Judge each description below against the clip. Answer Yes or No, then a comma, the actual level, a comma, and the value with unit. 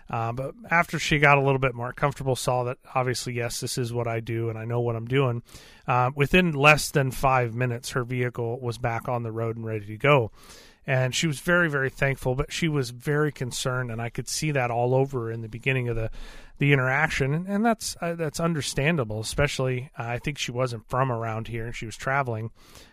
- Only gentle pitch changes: No, average, 3.2 semitones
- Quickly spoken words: Yes, fast, 230 wpm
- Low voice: Yes, low, 130 Hz